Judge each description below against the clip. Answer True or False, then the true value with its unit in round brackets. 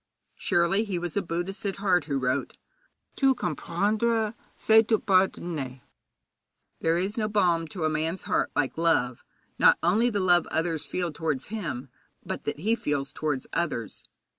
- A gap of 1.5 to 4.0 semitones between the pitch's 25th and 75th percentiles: False (4.8 semitones)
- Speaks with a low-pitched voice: False (175 Hz)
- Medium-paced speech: True (160 wpm)